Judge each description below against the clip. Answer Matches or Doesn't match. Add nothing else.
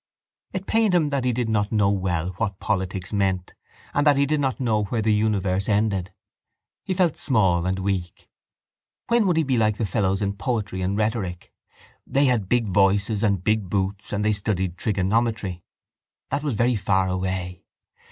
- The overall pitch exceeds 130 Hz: Doesn't match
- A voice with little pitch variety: Doesn't match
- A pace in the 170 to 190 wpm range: Matches